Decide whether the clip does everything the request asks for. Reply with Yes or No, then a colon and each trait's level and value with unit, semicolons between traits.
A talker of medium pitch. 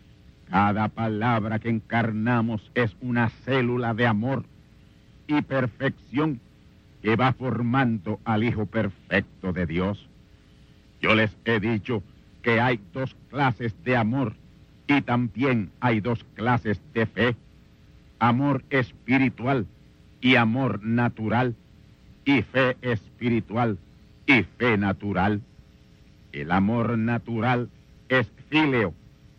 No: low, 115 Hz